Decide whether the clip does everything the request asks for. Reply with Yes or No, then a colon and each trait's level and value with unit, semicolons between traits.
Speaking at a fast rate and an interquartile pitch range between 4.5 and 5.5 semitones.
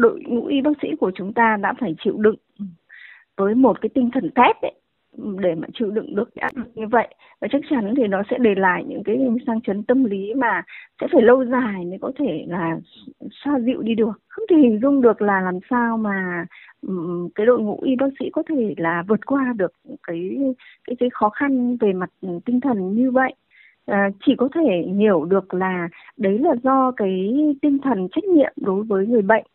No: average, 210 wpm; average, 5.2 semitones